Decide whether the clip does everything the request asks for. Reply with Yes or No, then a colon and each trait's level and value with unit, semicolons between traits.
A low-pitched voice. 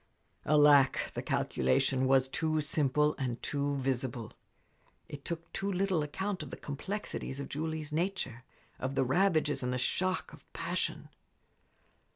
No: medium, 145 Hz